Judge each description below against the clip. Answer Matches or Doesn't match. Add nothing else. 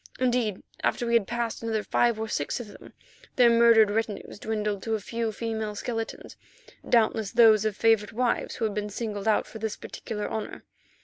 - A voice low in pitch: Doesn't match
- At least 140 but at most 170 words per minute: Doesn't match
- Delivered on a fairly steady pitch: Matches